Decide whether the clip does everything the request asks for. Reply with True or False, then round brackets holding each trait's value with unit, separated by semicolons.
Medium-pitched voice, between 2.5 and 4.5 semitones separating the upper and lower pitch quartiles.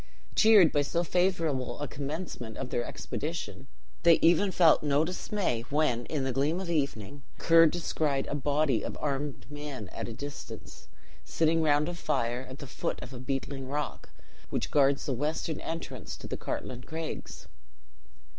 True (145 Hz; 3.4 semitones)